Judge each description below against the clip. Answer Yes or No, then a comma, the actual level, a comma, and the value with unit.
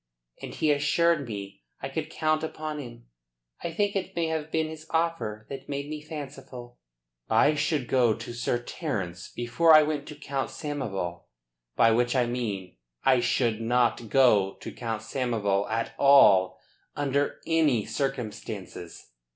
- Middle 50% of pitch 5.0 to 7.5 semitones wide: Yes, wide, 5.4 semitones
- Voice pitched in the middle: No, low, 130 Hz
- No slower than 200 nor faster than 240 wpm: No, average, 155 wpm